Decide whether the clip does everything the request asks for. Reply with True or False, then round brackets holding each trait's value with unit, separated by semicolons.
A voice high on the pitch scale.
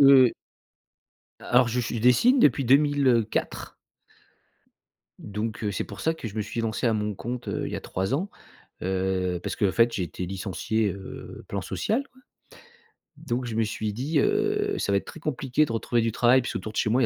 False (115 Hz)